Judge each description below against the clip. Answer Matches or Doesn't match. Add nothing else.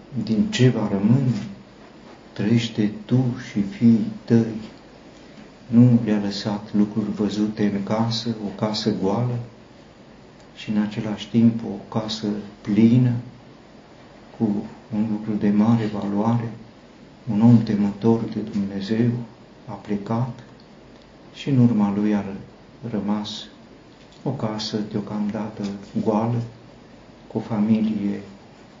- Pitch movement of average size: Doesn't match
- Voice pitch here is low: Matches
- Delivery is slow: Matches